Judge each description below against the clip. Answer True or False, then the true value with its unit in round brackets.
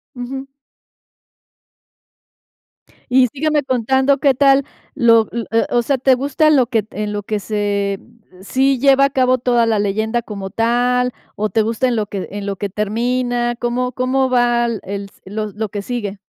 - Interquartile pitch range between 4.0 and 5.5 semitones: False (3.5 semitones)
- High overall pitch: True (240 Hz)